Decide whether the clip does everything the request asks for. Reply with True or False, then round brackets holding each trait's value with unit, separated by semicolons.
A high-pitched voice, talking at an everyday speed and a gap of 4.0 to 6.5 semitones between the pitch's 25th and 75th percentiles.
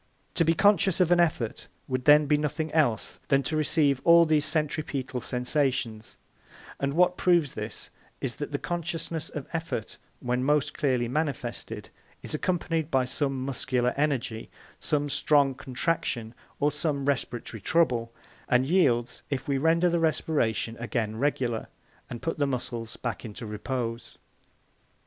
False (140 Hz; 145 wpm; 4.5 semitones)